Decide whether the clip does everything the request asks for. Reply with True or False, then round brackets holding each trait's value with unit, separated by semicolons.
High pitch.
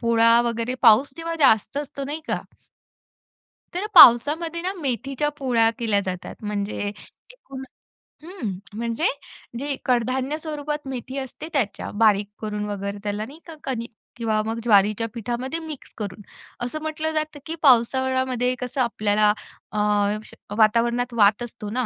True (245 Hz)